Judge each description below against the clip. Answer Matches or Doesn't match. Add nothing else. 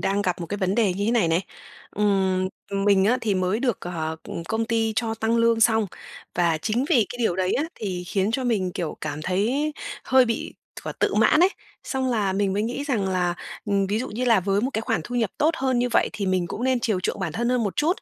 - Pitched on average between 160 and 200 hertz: Doesn't match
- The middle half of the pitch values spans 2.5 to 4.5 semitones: Matches